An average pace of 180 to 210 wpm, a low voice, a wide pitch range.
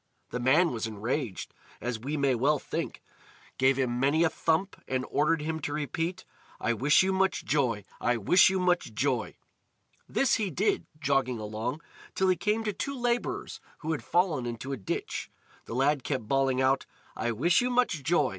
No: average, 185 wpm; medium, 145 Hz; wide, 6.1 semitones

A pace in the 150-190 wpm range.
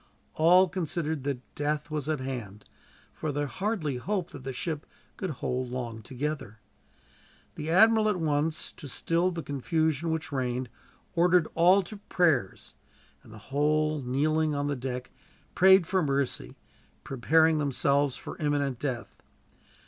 No: average, 140 wpm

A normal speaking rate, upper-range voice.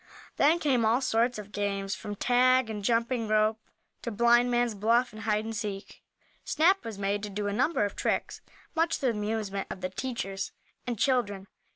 Yes: average, 185 wpm; high, 220 Hz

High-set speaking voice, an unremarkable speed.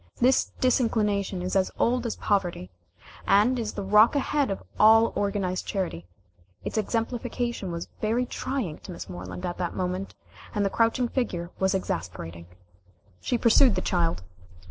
Yes: high, 200 Hz; average, 150 wpm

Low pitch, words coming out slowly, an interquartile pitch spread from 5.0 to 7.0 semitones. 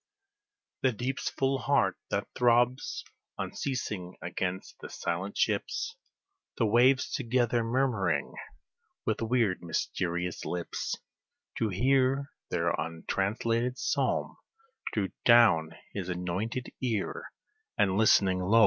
Yes: low, 110 Hz; slow, 105 wpm; wide, 5.5 semitones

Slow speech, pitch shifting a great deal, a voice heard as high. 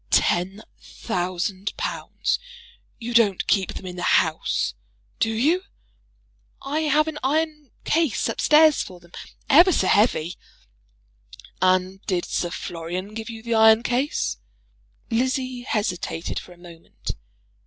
Yes: slow, 130 wpm; wide, 6.8 semitones; high, 220 Hz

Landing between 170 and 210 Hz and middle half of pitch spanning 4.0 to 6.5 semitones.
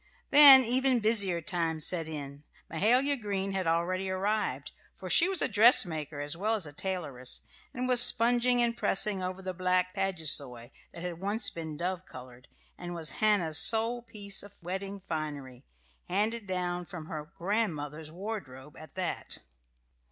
Yes: medium, 185 Hz; average, 5.1 semitones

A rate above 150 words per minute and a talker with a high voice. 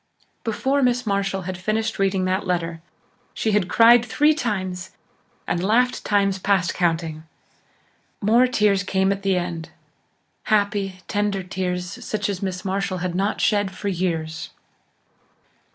No: slow, 135 wpm; high, 195 Hz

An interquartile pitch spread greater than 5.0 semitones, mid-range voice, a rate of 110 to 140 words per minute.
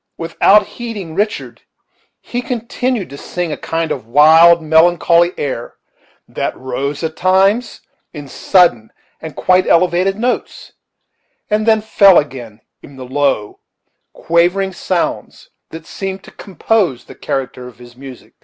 Yes: wide, 5.6 semitones; medium, 170 Hz; slow, 135 wpm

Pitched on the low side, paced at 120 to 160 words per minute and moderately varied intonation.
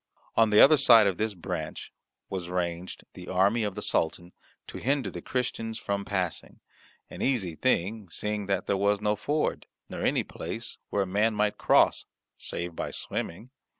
No: low, 100 Hz; average, 175 wpm; average, 3.6 semitones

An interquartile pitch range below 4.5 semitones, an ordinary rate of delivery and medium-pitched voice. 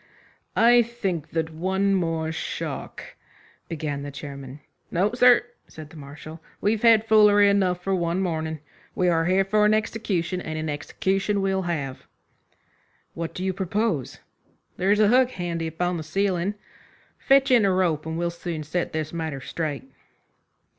Yes: average, 4.1 semitones; average, 160 wpm; medium, 180 Hz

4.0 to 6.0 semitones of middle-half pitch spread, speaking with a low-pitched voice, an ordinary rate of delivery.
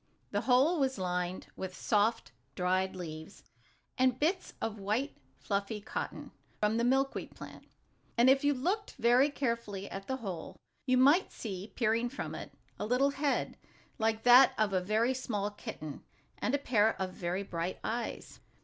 No: average, 5.0 semitones; high, 225 Hz; average, 160 wpm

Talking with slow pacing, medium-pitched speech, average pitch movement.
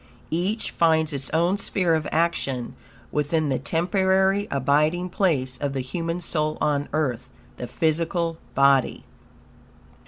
Yes: slow, 125 wpm; medium, 160 Hz; average, 3.8 semitones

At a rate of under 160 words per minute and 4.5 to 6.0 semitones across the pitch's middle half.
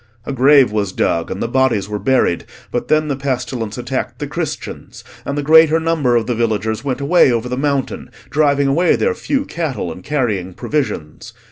No: average, 190 wpm; average, 4.8 semitones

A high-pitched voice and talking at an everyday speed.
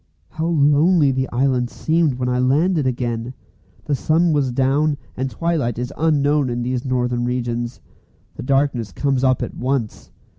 No: low, 130 Hz; average, 155 wpm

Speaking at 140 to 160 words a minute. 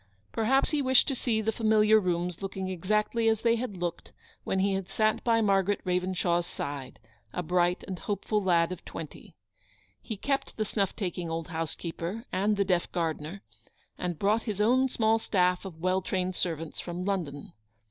No: average, 175 wpm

